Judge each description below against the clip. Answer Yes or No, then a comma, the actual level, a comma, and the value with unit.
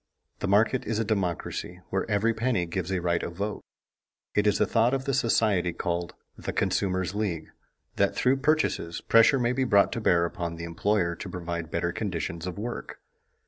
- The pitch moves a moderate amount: Yes, average, 4.7 semitones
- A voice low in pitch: Yes, low, 100 Hz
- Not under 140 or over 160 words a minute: No, average, 185 wpm